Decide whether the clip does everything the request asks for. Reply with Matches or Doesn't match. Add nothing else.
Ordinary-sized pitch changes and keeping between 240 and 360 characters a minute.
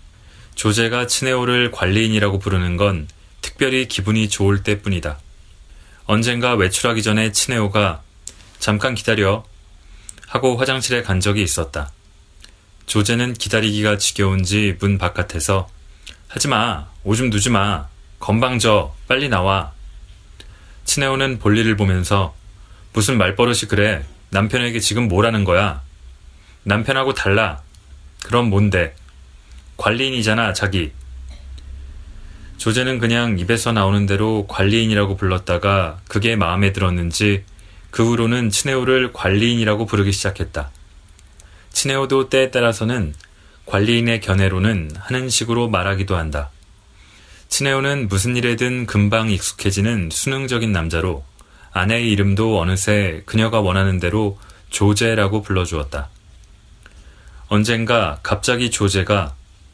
Matches